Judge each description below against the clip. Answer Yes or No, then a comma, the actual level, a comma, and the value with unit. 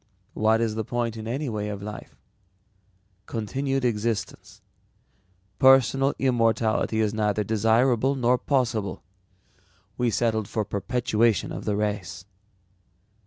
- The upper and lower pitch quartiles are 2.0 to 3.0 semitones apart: Yes, average, 2.7 semitones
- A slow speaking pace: Yes, slow, 115 wpm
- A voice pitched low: Yes, low, 110 Hz